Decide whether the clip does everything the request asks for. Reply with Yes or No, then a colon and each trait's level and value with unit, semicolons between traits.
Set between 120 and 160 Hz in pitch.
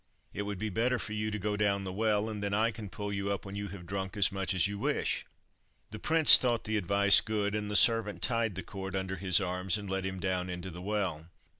No: low, 100 Hz